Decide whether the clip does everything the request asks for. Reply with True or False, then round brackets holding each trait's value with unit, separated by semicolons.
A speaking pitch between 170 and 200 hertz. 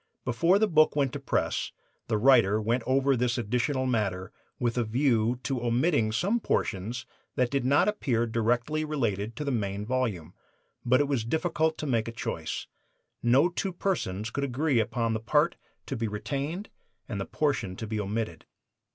False (125 Hz)